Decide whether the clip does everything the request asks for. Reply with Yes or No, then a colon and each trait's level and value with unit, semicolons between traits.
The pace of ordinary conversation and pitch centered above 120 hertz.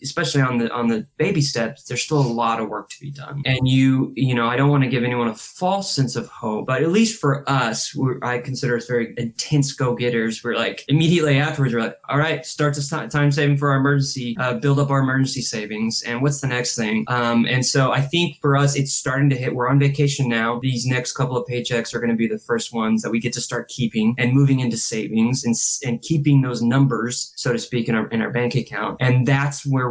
No: fast, 250 wpm; low, 130 Hz